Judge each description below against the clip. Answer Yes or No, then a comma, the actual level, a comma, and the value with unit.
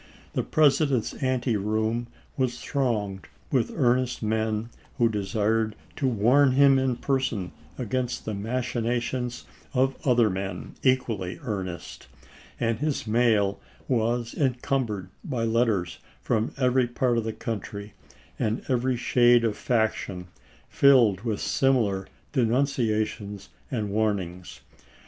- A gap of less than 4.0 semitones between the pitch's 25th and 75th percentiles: Yes, average, 3.2 semitones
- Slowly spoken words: Yes, slow, 115 wpm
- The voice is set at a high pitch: No, low, 115 Hz